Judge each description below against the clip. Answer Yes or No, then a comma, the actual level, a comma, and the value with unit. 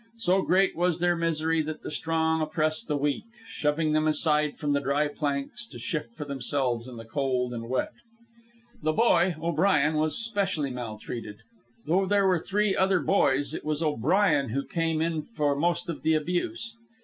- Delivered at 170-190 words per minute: Yes, average, 175 wpm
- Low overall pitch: No, medium, 155 Hz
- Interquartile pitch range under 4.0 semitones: Yes, average, 3.6 semitones